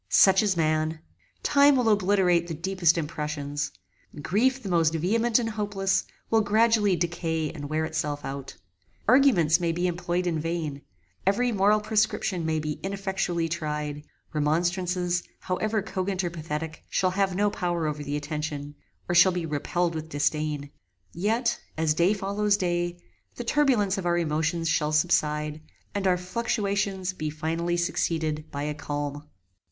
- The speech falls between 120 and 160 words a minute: Yes, average, 150 wpm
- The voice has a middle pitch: Yes, medium, 175 Hz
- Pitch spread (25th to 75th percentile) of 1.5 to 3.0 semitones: No, average, 4.1 semitones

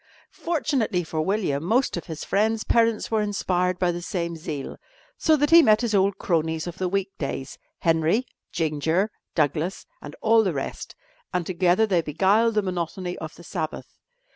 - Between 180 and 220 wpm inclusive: No, average, 170 wpm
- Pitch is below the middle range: No, medium, 180 Hz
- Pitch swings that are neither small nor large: Yes, average, 4.7 semitones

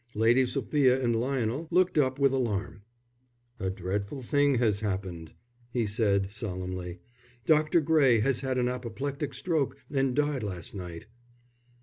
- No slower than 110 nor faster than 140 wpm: Yes, slow, 135 wpm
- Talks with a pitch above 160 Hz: No, low, 125 Hz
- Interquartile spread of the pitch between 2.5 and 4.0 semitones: No, wide, 5.4 semitones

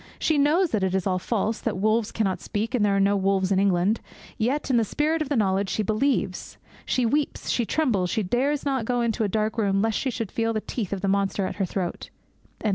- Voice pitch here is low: No, high, 215 Hz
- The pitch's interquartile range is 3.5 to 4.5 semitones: Yes, average, 4.1 semitones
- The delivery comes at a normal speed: No, fast, 235 wpm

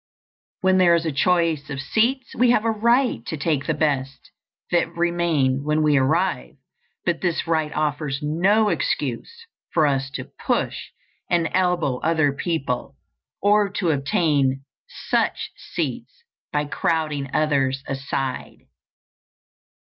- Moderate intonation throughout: Yes, average, 4.2 semitones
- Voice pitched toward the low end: No, medium, 155 Hz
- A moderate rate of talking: No, slow, 130 wpm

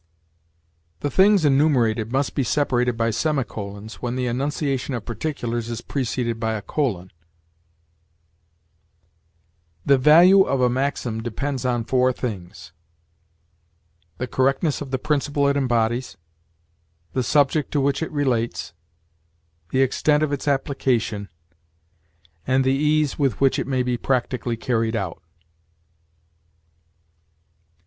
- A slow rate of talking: Yes, slow, 120 wpm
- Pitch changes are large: No, average, 3.4 semitones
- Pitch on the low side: Yes, low, 130 Hz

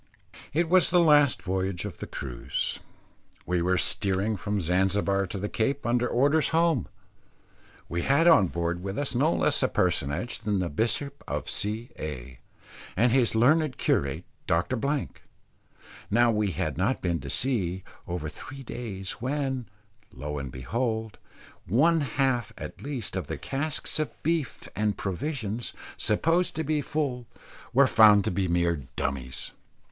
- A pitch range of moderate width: No, wide, 7.3 semitones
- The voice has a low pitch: Yes, low, 110 Hz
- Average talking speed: Yes, average, 150 wpm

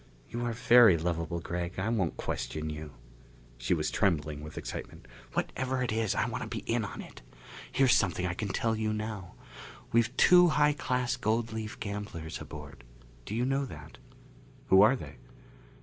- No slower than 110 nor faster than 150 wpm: No, average, 175 wpm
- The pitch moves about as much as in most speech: No, wide, 6.0 semitones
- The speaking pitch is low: Yes, low, 105 Hz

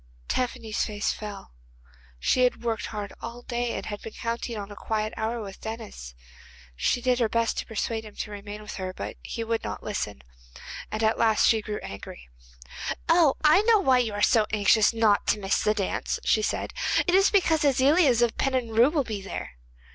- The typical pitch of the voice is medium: No, high, 225 Hz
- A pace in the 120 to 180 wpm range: No, average, 195 wpm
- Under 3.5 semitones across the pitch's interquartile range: Yes, average, 2.9 semitones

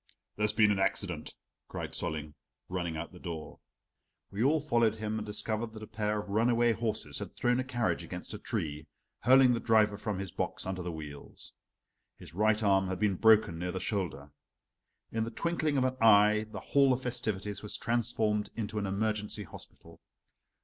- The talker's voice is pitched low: Yes, low, 105 Hz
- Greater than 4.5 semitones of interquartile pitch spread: No, average, 3.2 semitones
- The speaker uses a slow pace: No, average, 185 wpm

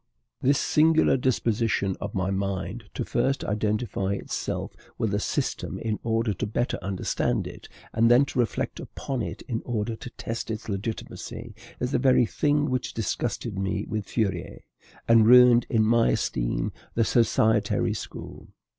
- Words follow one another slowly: No, average, 155 wpm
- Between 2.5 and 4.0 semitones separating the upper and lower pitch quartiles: Yes, average, 3.1 semitones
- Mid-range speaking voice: No, low, 115 Hz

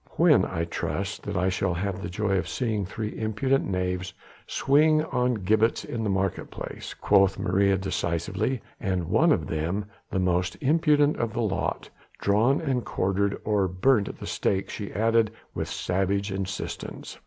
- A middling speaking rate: Yes, average, 165 wpm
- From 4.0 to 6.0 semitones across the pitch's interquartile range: No, average, 3.6 semitones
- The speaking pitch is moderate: No, low, 100 Hz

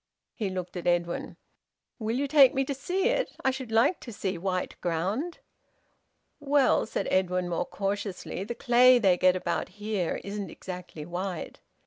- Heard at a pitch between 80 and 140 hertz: No, high, 200 Hz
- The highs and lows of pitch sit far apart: Yes, wide, 5.8 semitones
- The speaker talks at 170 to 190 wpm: No, average, 160 wpm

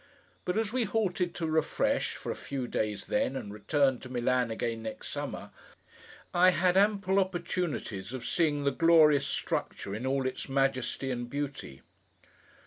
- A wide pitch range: Yes, wide, 6.4 semitones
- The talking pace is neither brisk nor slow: Yes, average, 155 wpm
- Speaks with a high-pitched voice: No, medium, 140 Hz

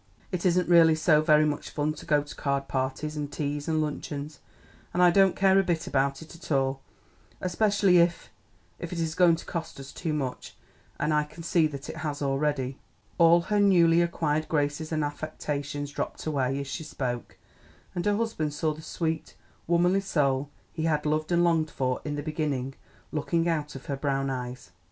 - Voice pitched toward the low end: No, medium, 155 Hz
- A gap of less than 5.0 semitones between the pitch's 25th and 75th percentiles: Yes, average, 2.9 semitones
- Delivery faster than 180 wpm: Yes, average, 195 wpm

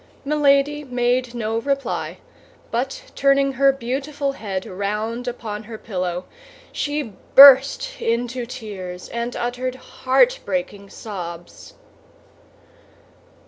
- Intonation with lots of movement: No, average, 4.4 semitones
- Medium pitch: No, high, 245 Hz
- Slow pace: Yes, slow, 95 wpm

